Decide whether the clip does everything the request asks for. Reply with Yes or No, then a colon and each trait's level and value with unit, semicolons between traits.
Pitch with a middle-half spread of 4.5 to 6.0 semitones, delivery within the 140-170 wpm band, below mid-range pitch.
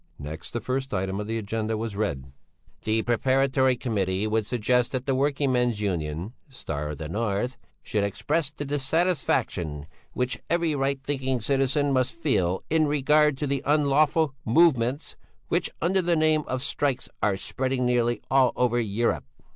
Yes: average, 4.9 semitones; average, 160 wpm; low, 125 Hz